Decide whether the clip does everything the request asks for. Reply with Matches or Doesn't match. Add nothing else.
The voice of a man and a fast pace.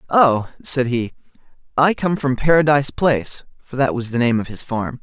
Doesn't match